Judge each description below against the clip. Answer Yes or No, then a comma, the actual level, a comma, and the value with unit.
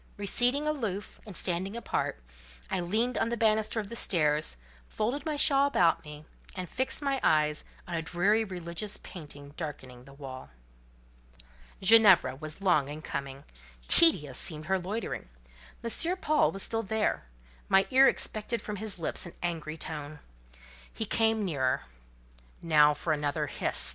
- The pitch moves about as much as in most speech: No, wide, 6.6 semitones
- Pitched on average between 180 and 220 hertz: Yes, medium, 185 Hz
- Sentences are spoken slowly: No, average, 150 wpm